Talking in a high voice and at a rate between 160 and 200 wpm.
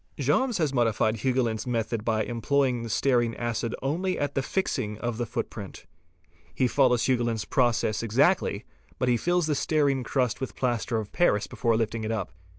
No: low, 120 Hz; average, 180 wpm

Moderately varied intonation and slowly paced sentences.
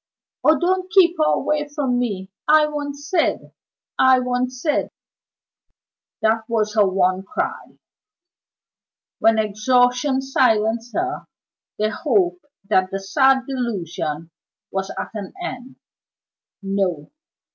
No: wide, 6.1 semitones; slow, 115 wpm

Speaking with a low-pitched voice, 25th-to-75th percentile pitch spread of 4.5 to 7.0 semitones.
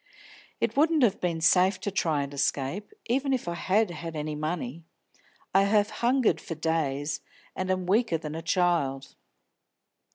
No: medium, 175 Hz; average, 4.9 semitones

